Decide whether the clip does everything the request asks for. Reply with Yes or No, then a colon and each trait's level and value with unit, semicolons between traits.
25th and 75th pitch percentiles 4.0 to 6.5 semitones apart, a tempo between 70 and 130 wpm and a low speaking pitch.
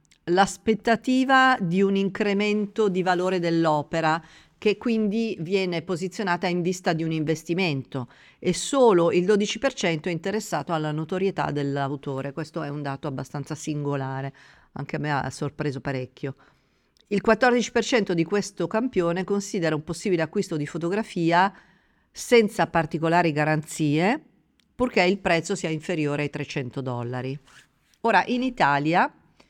No: average, 5.0 semitones; average, 125 wpm; medium, 170 Hz